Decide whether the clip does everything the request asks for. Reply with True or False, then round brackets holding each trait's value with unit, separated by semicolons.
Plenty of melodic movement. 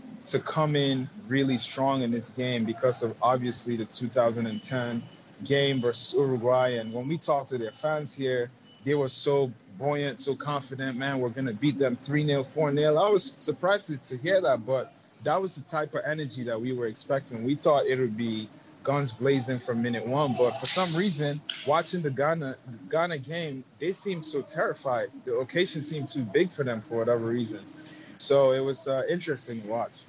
False (3.6 semitones)